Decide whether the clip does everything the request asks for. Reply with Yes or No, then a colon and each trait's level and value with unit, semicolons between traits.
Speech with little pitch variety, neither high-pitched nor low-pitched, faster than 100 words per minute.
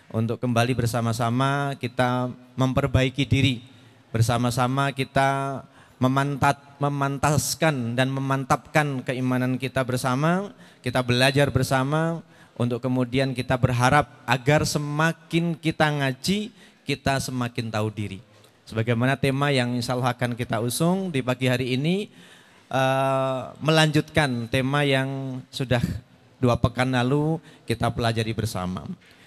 No: narrow, 2.3 semitones; low, 130 Hz; average, 110 wpm